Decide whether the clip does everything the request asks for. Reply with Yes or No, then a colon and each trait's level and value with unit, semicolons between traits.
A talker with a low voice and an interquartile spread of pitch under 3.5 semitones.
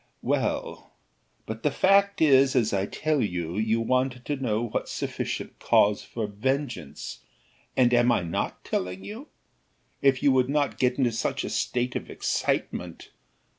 No: low, 125 Hz; average, 4.0 semitones